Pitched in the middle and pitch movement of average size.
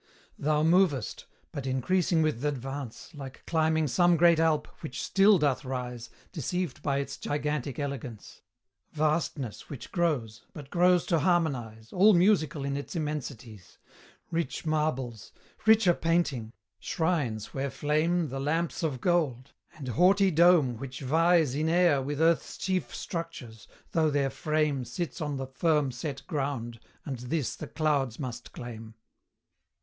Yes: medium, 150 Hz; average, 4.2 semitones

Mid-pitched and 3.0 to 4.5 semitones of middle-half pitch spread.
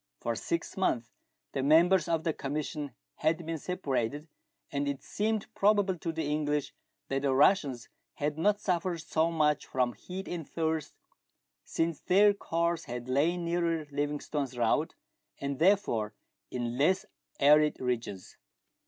Yes: medium, 155 Hz; average, 3.8 semitones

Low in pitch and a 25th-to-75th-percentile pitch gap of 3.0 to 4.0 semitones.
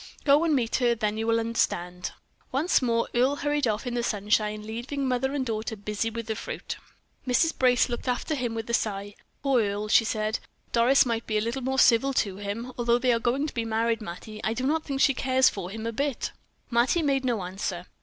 No: high, 235 Hz; average, 3.3 semitones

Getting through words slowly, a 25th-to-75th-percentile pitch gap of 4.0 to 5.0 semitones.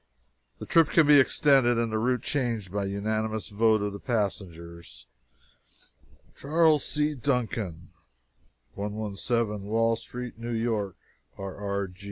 No: slow, 125 wpm; average, 3.6 semitones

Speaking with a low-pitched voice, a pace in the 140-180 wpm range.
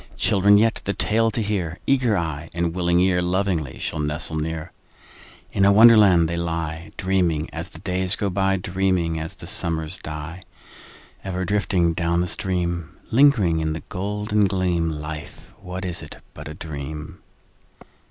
Yes: very low, 90 Hz; average, 160 wpm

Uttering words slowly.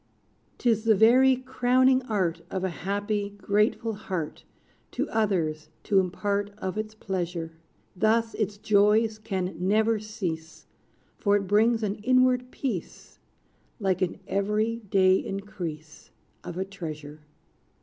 Yes: slow, 125 wpm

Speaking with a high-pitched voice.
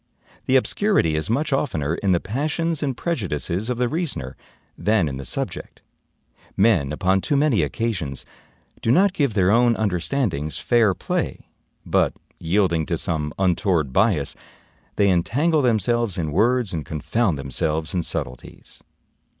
No: low, 100 Hz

